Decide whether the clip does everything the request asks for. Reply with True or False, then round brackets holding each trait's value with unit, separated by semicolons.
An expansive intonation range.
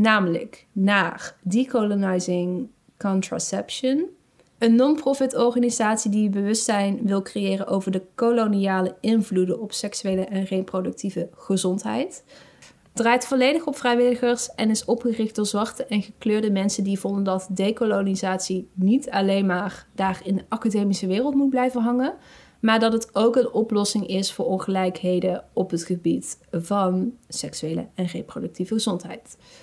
False (3.6 semitones)